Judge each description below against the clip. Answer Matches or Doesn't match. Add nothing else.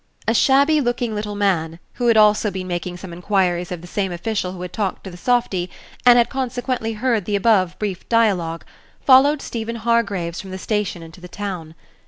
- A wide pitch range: Doesn't match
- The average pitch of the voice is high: Matches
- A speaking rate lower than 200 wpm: Doesn't match